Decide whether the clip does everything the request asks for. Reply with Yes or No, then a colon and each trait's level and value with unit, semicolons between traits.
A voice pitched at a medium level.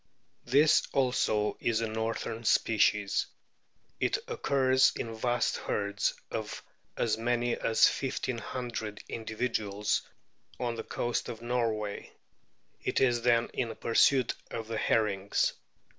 No: low, 115 Hz